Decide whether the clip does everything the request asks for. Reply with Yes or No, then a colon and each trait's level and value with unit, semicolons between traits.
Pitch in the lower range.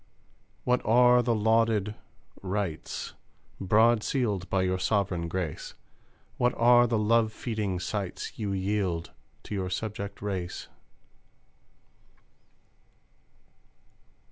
Yes: low, 105 Hz